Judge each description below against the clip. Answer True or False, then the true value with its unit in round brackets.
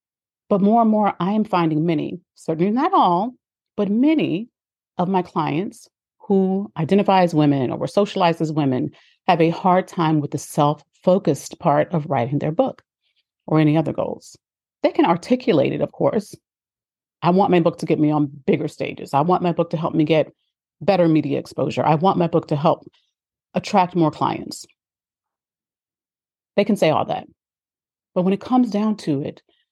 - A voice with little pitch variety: False (4.3 semitones)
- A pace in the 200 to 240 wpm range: False (180 wpm)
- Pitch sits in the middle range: True (175 Hz)